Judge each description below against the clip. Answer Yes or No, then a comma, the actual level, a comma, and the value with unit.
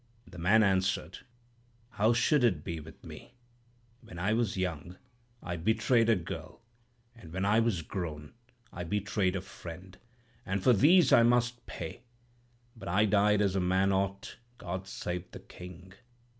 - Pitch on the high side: No, very low, 95 Hz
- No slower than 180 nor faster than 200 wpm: No, average, 155 wpm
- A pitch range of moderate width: Yes, average, 3.7 semitones